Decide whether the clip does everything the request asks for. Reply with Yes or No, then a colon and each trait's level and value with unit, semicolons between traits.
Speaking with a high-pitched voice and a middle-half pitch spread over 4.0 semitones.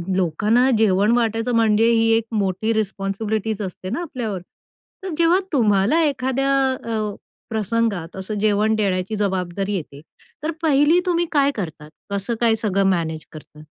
No: high, 215 Hz; average, 3.5 semitones